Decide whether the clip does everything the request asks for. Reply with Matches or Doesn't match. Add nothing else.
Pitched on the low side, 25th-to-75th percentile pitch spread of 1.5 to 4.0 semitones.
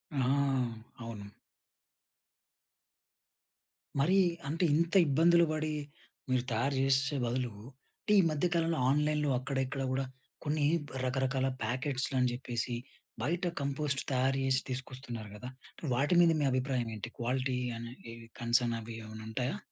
Matches